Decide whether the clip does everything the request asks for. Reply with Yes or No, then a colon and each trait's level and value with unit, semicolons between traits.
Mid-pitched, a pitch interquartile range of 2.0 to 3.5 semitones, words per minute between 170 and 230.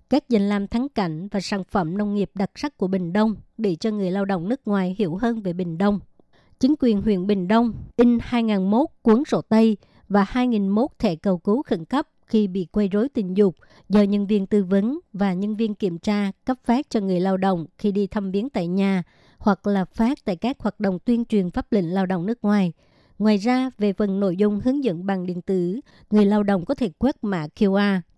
No: high, 205 Hz; average, 2.9 semitones; average, 225 wpm